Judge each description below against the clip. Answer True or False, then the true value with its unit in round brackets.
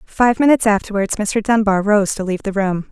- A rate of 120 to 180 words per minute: False (205 wpm)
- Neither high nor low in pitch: False (205 Hz)